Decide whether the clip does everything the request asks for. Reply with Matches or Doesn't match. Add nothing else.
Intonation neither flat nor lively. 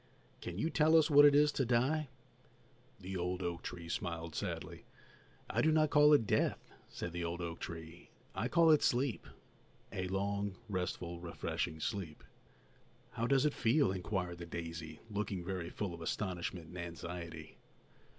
Doesn't match